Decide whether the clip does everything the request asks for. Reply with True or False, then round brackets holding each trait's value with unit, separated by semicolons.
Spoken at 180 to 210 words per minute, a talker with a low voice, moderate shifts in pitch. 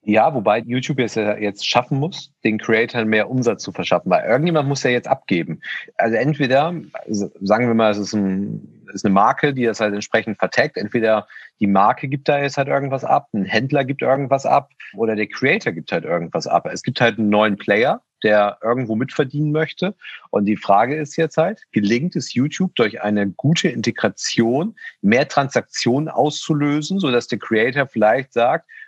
False (190 wpm; 125 Hz; 5.7 semitones)